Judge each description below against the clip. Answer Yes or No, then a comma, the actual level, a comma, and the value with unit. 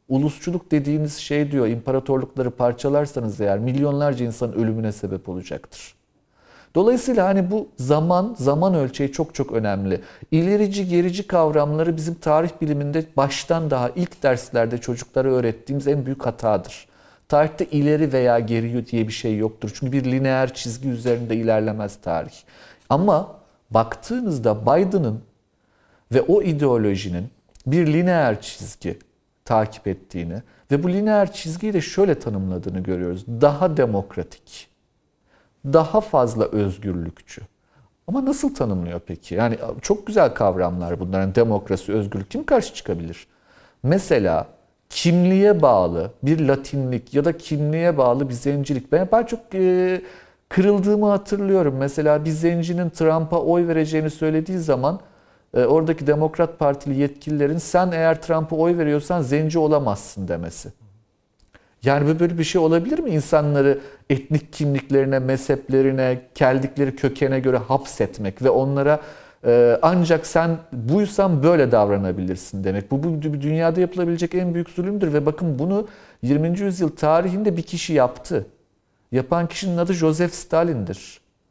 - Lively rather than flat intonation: Yes, wide, 6.4 semitones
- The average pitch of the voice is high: No, medium, 140 Hz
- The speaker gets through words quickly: No, average, 125 wpm